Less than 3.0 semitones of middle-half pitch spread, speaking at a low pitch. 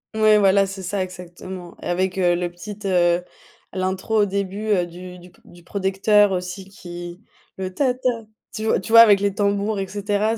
No: narrow, 2.4 semitones; high, 190 Hz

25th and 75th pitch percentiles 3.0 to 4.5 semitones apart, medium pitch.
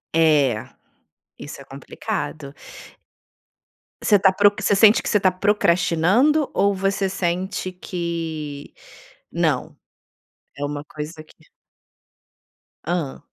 Yes: average, 4.2 semitones; medium, 175 Hz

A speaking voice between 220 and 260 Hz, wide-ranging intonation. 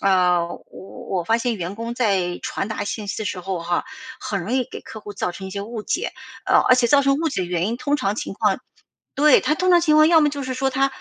Yes: high, 225 Hz; wide, 6.2 semitones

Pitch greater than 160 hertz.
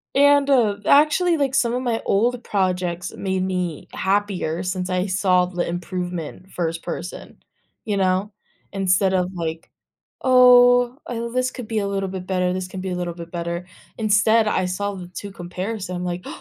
Yes: high, 190 Hz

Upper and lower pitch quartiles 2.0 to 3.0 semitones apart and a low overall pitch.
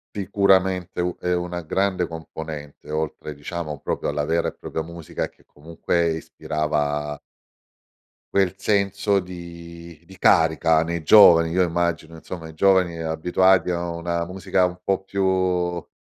Yes: narrow, 2.4 semitones; very low, 85 Hz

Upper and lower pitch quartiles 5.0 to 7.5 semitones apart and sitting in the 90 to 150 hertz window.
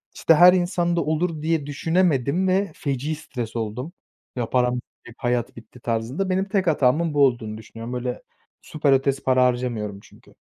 Yes: average, 5.3 semitones; low, 135 Hz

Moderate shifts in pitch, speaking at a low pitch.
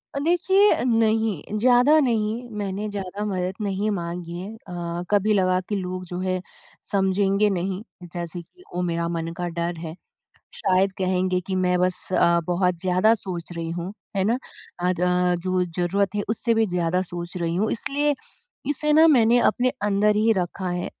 No: average, 3.3 semitones; high, 190 Hz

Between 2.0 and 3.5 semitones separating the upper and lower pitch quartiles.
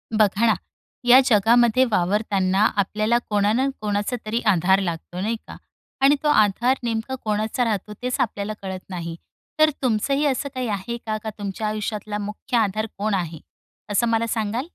Yes: average, 2.9 semitones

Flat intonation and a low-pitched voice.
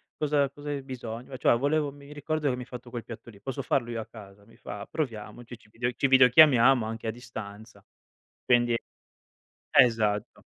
No: average, 3.4 semitones; low, 120 Hz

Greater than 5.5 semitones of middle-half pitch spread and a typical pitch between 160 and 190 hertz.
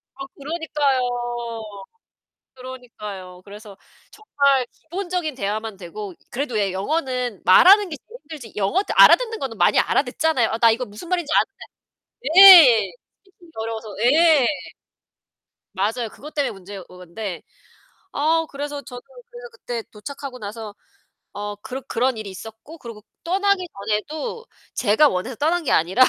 No: wide, 7.1 semitones; very high, 255 Hz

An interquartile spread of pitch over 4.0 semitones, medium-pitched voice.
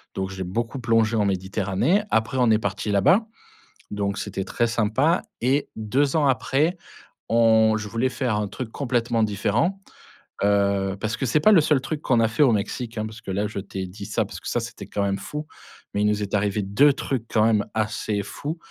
No: average, 4.4 semitones; low, 110 Hz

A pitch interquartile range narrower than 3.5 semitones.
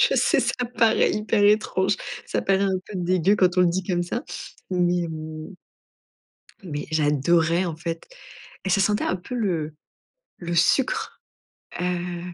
Yes: average, 2.8 semitones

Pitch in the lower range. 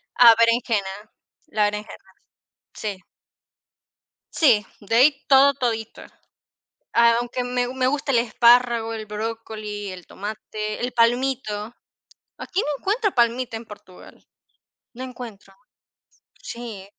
No: high, 230 Hz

